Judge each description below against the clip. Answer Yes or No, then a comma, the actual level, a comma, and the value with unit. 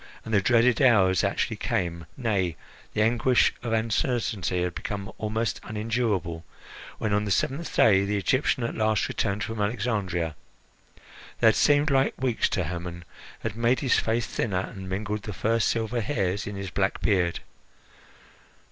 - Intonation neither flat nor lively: Yes, average, 3.4 semitones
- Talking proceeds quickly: No, average, 155 wpm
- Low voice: Yes, low, 105 Hz